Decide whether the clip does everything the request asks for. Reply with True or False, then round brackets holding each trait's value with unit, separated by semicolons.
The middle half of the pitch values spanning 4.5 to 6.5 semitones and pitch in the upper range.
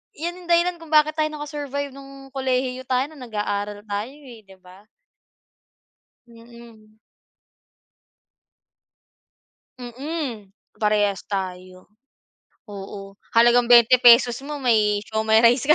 True (4.8 semitones; 240 Hz)